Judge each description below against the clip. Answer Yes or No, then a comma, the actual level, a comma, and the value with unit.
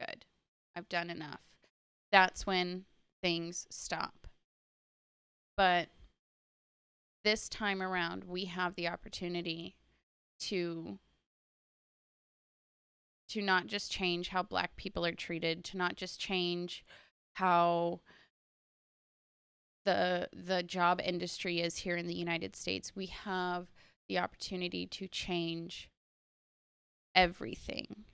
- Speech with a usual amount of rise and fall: No, narrow, 1.5 semitones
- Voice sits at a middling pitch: Yes, medium, 175 Hz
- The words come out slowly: Yes, slow, 100 wpm